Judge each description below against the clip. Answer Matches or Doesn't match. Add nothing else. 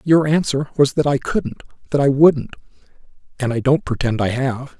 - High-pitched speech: Doesn't match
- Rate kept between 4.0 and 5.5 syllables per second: Matches